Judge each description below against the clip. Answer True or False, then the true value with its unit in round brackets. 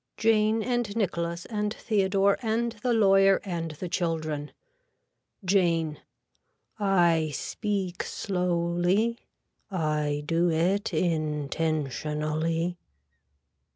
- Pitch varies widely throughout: False (3.9 semitones)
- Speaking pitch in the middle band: True (175 Hz)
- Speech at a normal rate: False (85 wpm)